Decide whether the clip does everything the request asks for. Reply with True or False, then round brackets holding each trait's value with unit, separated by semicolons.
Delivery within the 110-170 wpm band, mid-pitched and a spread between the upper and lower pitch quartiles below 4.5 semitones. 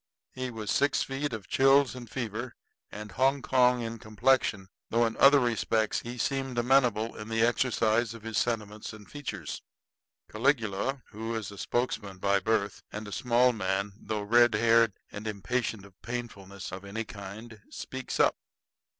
False (160 wpm; 115 Hz; 2.9 semitones)